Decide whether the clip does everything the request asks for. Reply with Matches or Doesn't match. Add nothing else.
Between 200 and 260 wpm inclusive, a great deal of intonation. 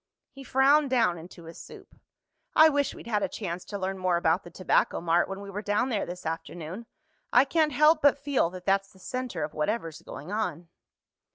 Matches